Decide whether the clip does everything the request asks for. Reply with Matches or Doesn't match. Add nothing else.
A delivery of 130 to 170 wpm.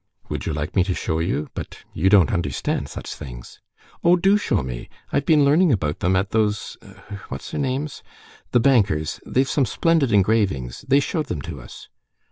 Doesn't match